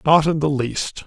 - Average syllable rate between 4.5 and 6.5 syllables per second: No, 4.2 syllables/s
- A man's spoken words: Yes, male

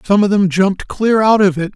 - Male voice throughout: Yes, male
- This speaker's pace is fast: Yes, fast, 275 wpm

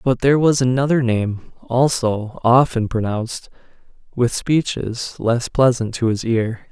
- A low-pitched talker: Yes, low, 120 Hz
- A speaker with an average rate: No, slow, 125 wpm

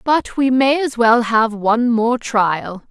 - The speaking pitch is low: No, high, 235 Hz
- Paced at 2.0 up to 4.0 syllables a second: Yes, 3.6 syllables/s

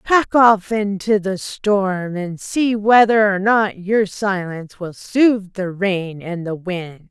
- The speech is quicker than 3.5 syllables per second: No, 3.4 syllables/s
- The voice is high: Yes, high, 200 Hz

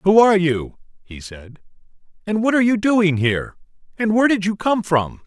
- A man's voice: Yes, male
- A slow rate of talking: No, average, 195 wpm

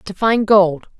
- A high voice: Yes, high, 200 Hz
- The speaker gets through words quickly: No, average, 180 wpm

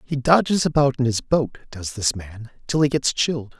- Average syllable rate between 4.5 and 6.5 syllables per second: Yes, 5.0 syllables/s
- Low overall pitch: Yes, low, 130 Hz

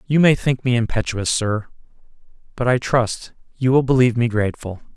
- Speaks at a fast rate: No, average, 170 wpm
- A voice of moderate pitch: No, low, 120 Hz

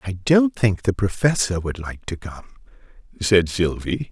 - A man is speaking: Yes, male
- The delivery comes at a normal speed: Yes, average, 160 wpm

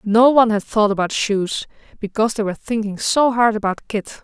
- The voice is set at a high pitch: Yes, high, 215 Hz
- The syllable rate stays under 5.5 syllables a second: No, 5.6 syllables/s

